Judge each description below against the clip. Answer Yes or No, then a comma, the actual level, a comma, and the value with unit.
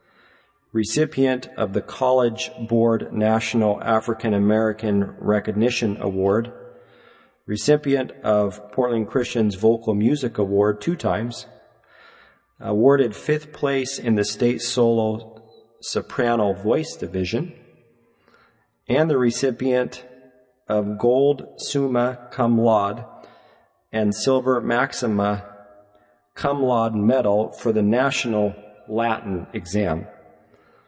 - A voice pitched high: No, low, 115 Hz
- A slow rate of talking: Yes, slow, 95 wpm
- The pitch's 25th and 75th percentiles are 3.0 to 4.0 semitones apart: Yes, average, 3.3 semitones